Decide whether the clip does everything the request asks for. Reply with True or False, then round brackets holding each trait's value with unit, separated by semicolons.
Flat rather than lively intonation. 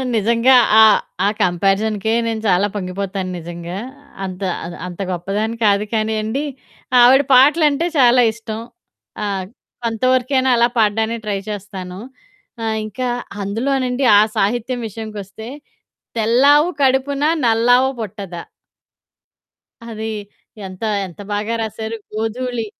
False (3.7 semitones)